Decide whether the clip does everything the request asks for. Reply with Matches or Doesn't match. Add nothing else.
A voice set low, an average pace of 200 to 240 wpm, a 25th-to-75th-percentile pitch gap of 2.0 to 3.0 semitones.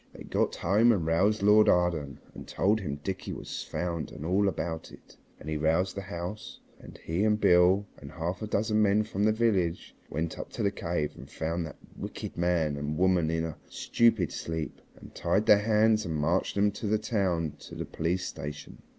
Doesn't match